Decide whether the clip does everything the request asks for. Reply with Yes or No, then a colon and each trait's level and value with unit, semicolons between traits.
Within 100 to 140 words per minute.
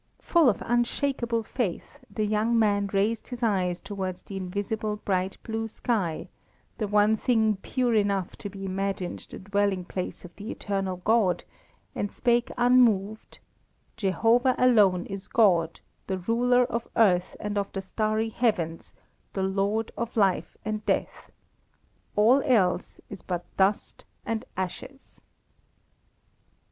Yes: slow, 135 wpm